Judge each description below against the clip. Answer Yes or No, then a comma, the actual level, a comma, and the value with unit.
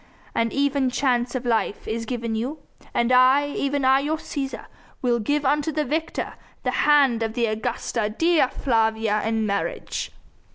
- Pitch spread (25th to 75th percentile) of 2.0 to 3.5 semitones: No, average, 4.0 semitones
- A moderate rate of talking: Yes, average, 160 wpm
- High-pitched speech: Yes, very high, 250 Hz